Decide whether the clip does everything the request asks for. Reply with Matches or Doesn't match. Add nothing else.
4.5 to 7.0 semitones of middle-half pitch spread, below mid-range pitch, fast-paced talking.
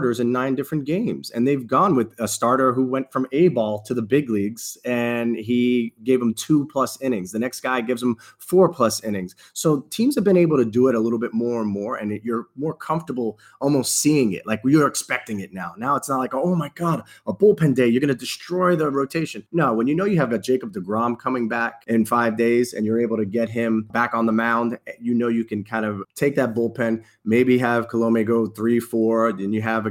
Doesn't match